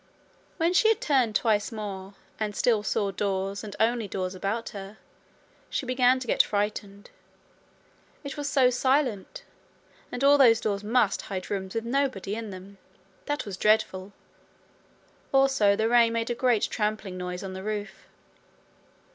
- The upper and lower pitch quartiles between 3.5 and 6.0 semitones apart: Yes, average, 4.0 semitones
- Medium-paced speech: Yes, average, 155 wpm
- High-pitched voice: Yes, high, 215 Hz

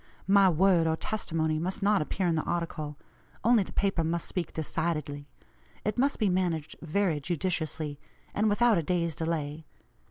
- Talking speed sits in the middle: Yes, average, 160 wpm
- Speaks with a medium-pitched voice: Yes, medium, 170 Hz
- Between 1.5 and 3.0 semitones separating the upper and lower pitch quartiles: No, average, 3.6 semitones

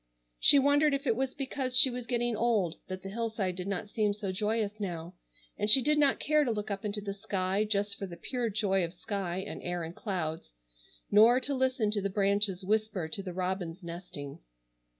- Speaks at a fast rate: Yes, fast, 210 wpm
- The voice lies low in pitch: No, high, 205 Hz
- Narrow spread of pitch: No, average, 4.0 semitones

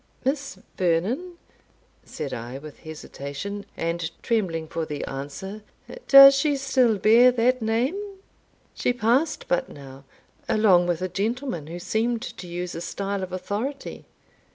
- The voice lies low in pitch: No, high, 200 Hz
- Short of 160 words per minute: Yes, slow, 135 wpm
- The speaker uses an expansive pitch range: Yes, wide, 7.1 semitones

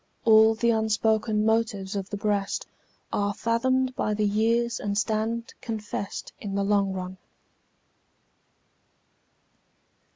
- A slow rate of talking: Yes, slow, 110 wpm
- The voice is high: Yes, high, 215 Hz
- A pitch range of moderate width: No, narrow, 2.1 semitones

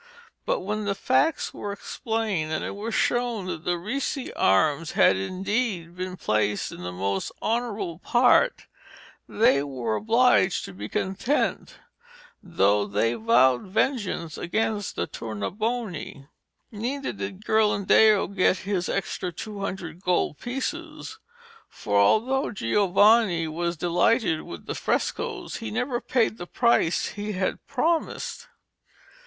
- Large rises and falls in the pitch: Yes, wide, 6.1 semitones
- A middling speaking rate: No, slow, 125 wpm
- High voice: Yes, high, 195 Hz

